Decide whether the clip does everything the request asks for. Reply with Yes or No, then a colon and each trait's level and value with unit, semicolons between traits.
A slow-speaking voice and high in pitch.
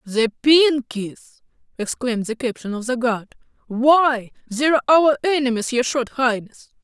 Yes: slow, 130 wpm; very high, 255 Hz